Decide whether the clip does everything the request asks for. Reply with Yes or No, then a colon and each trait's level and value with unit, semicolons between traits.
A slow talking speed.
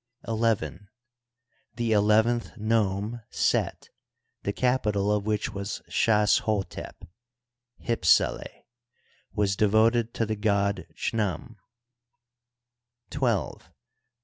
Yes: slow, 90 wpm